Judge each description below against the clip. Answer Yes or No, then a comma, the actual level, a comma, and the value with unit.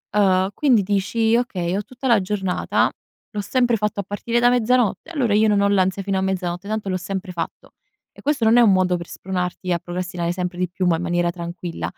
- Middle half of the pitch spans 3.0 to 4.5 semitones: Yes, average, 3.4 semitones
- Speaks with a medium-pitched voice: No, high, 195 Hz